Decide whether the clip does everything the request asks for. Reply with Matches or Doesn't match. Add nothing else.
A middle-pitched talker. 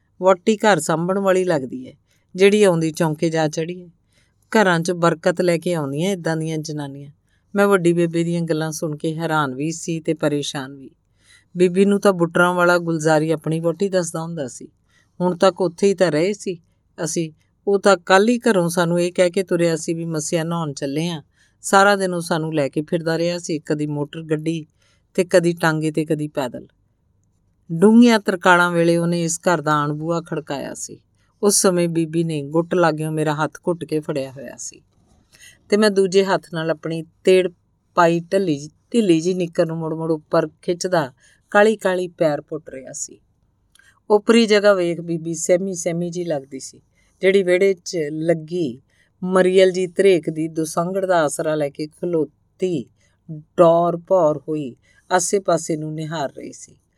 Matches